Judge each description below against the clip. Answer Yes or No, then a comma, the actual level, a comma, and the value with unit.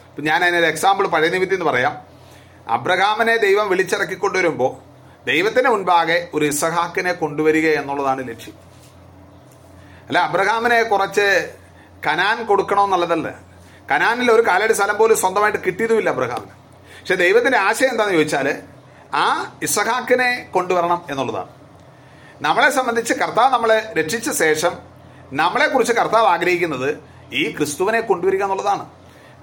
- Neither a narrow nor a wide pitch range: No, wide, 6.6 semitones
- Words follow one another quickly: No, average, 110 wpm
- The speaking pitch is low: No, medium, 180 Hz